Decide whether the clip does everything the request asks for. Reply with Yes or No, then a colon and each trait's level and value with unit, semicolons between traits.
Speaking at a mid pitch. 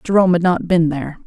Yes: medium, 170 Hz